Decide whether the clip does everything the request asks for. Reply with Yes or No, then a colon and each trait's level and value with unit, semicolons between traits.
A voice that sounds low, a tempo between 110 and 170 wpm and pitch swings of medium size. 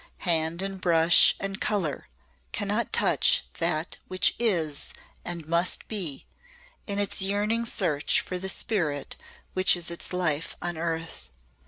No: medium, 175 Hz; slow, 135 wpm; average, 3.1 semitones